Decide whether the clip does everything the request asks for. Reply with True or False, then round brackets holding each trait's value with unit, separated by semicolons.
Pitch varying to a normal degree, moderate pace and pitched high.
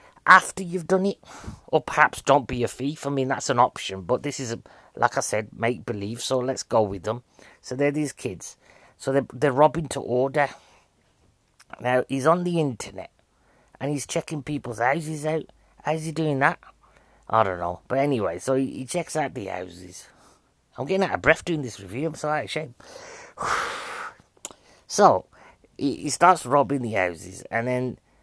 False (4.8 semitones; 185 wpm; 135 Hz)